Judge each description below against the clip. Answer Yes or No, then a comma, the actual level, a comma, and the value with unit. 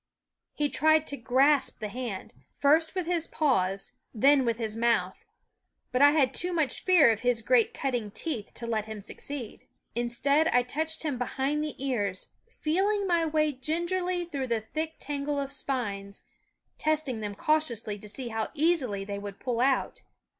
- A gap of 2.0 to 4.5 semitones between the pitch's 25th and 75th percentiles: No, average, 5.3 semitones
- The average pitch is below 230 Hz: No, very high, 270 Hz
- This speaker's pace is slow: No, average, 170 wpm